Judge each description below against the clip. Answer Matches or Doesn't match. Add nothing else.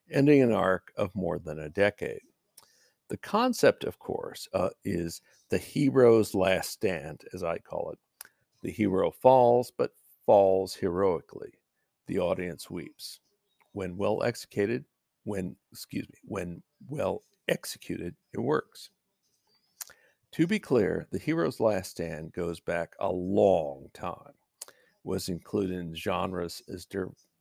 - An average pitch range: Doesn't match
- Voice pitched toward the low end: Matches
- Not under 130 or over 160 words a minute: Matches